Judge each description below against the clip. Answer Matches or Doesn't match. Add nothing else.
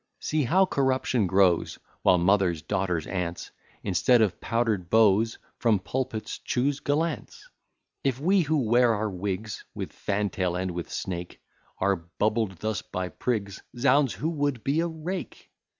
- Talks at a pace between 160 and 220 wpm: Doesn't match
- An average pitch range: Doesn't match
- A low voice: Matches